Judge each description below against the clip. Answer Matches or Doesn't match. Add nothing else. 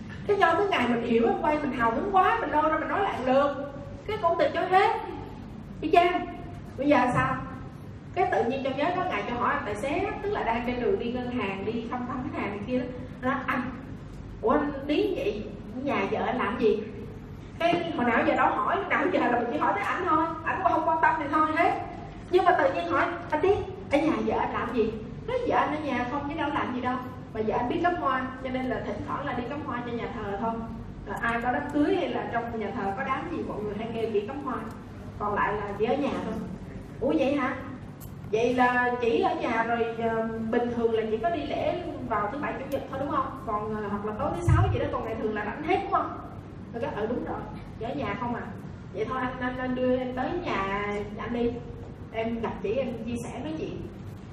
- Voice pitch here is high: Matches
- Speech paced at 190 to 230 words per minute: Doesn't match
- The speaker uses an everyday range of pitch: Doesn't match